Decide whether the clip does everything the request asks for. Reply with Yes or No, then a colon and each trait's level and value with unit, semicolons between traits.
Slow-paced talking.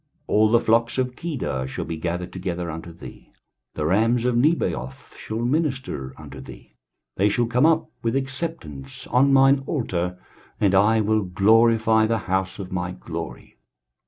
No: average, 160 wpm